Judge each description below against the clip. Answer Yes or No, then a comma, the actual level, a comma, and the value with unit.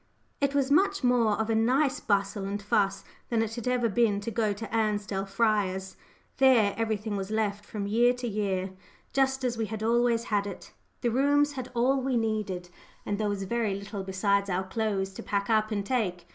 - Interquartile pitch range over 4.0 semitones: No, average, 3.2 semitones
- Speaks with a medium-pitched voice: No, high, 215 Hz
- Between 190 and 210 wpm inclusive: Yes, average, 200 wpm